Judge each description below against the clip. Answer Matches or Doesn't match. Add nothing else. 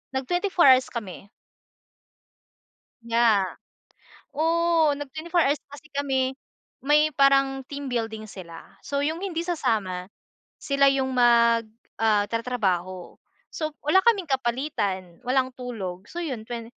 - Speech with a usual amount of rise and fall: Matches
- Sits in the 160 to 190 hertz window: Doesn't match